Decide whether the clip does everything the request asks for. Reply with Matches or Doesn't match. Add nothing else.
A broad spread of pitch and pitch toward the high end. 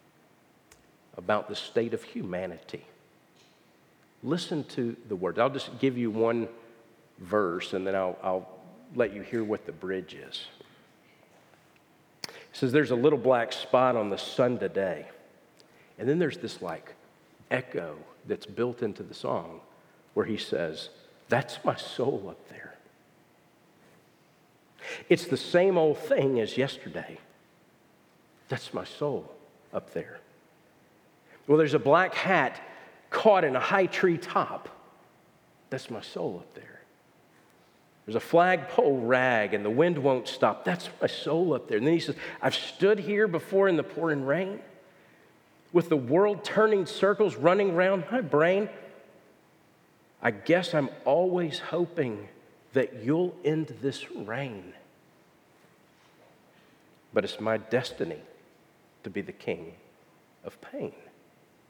Doesn't match